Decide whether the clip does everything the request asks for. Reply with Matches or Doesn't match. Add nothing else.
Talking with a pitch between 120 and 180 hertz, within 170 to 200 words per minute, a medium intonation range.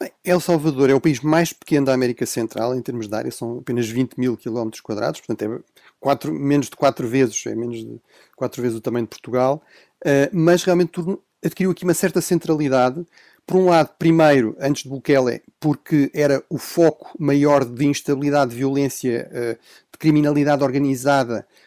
Matches